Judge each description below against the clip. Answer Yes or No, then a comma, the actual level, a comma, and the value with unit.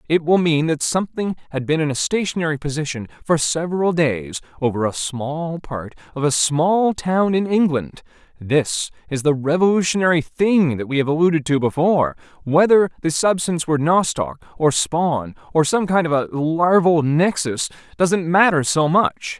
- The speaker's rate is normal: Yes, average, 165 wpm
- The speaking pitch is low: No, medium, 160 Hz